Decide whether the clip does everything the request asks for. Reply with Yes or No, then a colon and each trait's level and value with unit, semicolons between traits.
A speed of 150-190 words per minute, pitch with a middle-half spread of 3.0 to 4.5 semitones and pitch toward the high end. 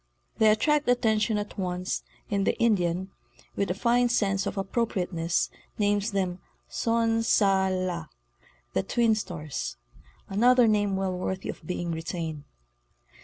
No: slow, 135 wpm; average, 3.6 semitones; high, 195 Hz